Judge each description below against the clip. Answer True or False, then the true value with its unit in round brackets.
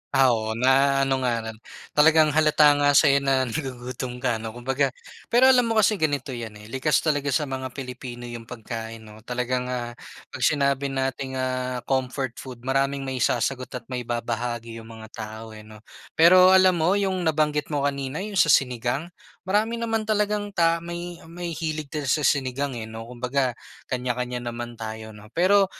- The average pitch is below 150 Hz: True (135 Hz)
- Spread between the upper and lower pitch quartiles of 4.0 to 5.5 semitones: True (4.4 semitones)